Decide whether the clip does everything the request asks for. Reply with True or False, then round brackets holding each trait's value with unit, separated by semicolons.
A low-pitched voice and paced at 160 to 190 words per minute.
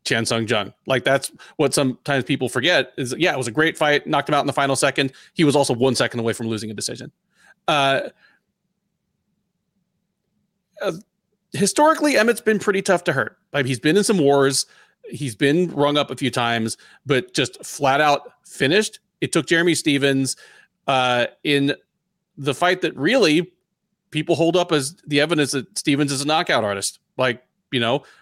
False (145 Hz; 180 wpm)